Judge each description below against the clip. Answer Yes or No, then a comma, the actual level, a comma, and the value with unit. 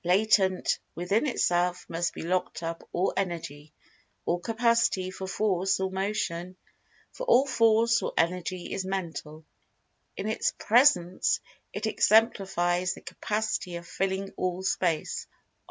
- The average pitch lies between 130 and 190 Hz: Yes, medium, 185 Hz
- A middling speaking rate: No, slow, 130 wpm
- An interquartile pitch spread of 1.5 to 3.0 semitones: No, average, 3.5 semitones